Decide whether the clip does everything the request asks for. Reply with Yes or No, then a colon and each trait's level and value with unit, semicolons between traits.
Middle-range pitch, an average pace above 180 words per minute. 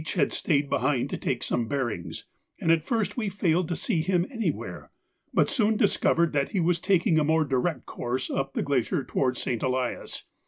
Yes: medium, 155 Hz; average, 190 wpm